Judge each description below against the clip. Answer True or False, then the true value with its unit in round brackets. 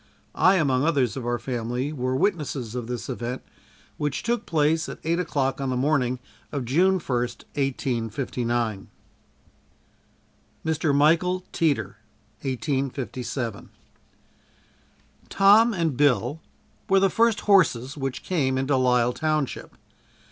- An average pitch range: True (4.4 semitones)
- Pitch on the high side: False (135 Hz)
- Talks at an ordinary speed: False (120 wpm)